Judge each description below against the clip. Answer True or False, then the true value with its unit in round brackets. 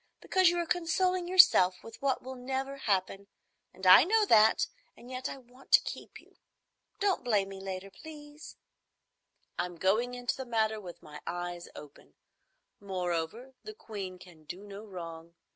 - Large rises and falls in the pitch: True (6.7 semitones)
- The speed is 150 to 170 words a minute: True (160 wpm)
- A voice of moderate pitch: False (220 Hz)